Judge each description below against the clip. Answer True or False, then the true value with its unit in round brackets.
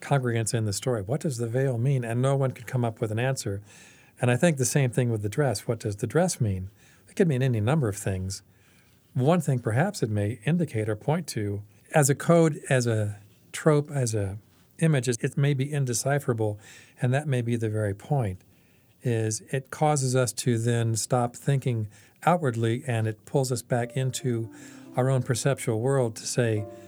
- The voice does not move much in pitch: False (3.7 semitones)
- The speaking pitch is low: True (125 Hz)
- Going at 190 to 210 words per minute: True (200 wpm)